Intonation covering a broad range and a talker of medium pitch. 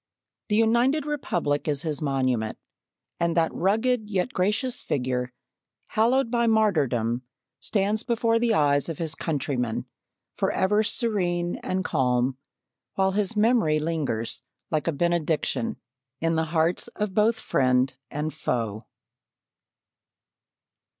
Yes: wide, 7.3 semitones; medium, 170 Hz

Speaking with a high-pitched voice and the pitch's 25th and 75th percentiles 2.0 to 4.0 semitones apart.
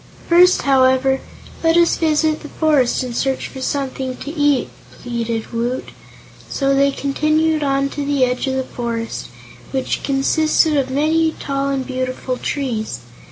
Yes: very high, 275 Hz; average, 2.8 semitones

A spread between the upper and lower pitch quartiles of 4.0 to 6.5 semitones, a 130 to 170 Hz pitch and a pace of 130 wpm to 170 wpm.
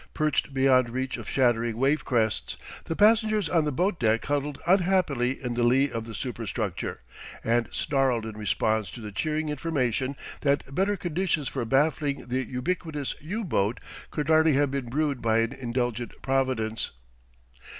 Yes: average, 4.4 semitones; low, 135 Hz; average, 155 wpm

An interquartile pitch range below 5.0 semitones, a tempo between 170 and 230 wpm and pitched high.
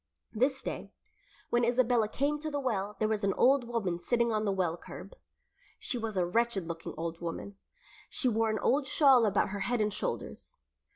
Yes: average, 4.2 semitones; average, 190 wpm; high, 220 Hz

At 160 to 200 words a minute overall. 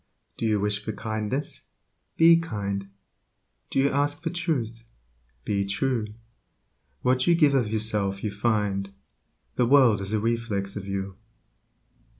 No: average, 140 wpm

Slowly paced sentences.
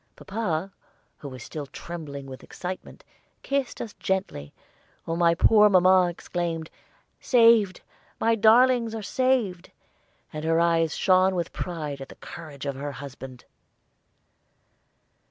Yes: slow, 125 wpm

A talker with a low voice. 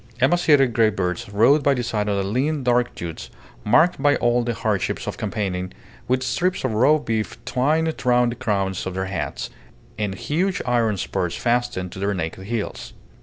Yes: low, 120 Hz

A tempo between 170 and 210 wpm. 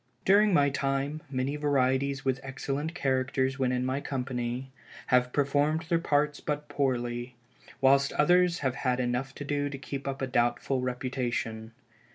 No: average, 160 wpm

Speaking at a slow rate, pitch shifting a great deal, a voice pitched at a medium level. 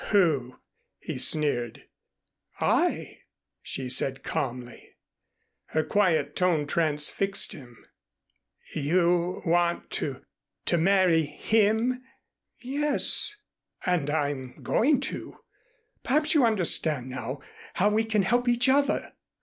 Yes: slow, 100 wpm; wide, 7.1 semitones; medium, 175 Hz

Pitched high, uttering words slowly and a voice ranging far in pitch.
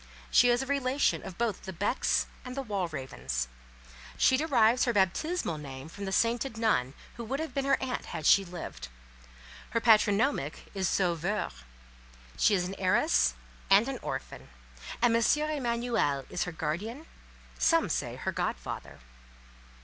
No: high, 215 Hz; average, 150 wpm; wide, 6.6 semitones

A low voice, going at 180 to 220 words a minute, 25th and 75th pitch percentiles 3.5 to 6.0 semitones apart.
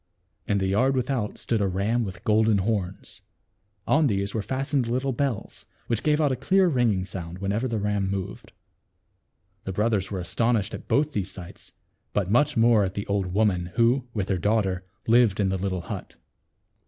Yes: low, 105 Hz; average, 185 wpm; average, 4.1 semitones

